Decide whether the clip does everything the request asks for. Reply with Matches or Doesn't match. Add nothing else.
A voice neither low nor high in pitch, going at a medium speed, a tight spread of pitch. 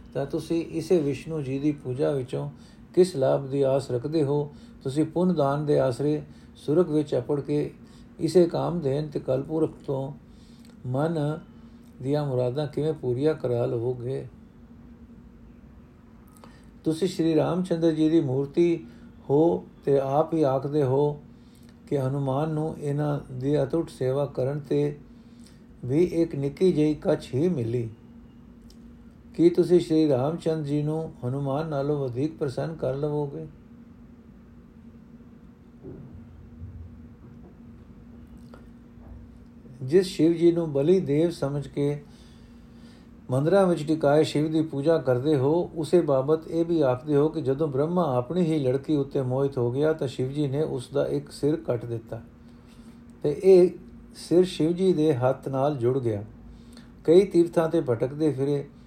Doesn't match